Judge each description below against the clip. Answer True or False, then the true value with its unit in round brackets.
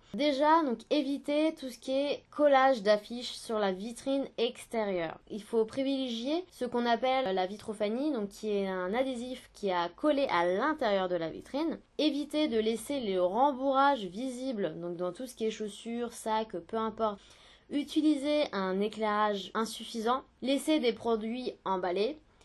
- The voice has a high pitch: True (235 Hz)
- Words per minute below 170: True (155 wpm)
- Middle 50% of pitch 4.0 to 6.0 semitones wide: True (4.7 semitones)